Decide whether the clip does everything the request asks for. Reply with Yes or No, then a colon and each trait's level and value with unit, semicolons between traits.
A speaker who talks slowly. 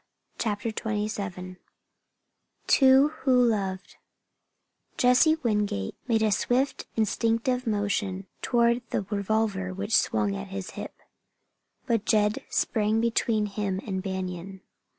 Yes: slow, 110 wpm